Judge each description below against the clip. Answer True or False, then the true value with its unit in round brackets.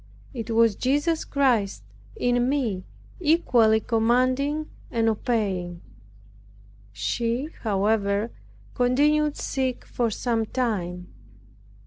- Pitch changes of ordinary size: True (3.6 semitones)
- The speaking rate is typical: False (80 wpm)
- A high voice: True (235 Hz)